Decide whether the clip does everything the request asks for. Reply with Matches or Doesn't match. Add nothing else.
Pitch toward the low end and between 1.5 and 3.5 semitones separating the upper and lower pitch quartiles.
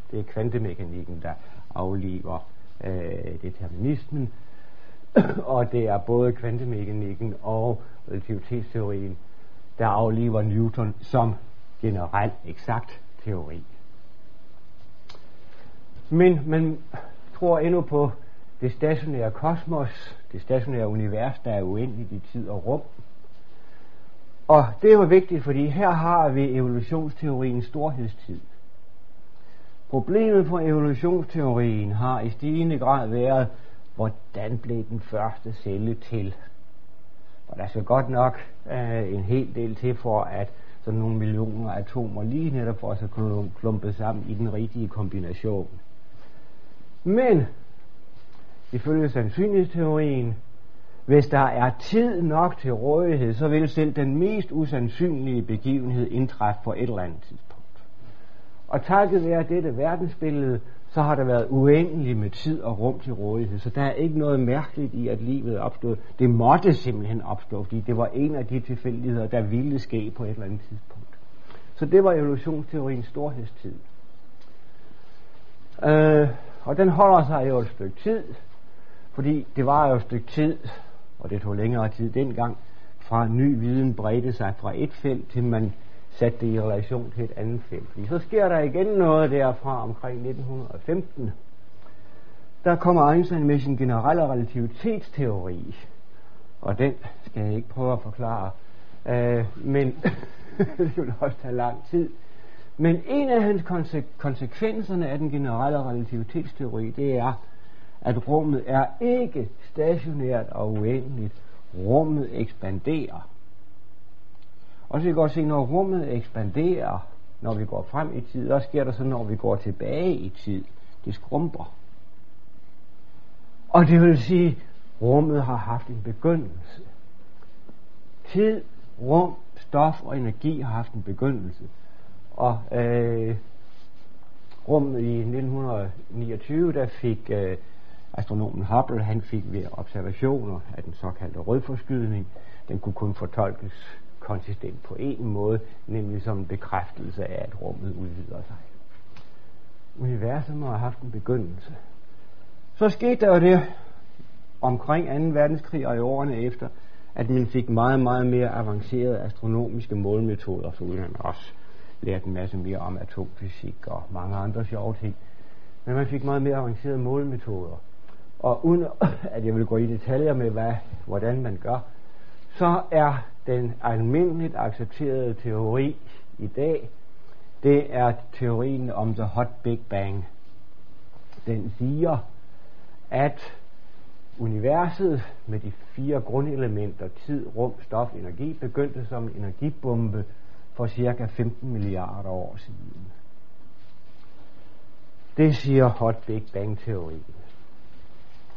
Doesn't match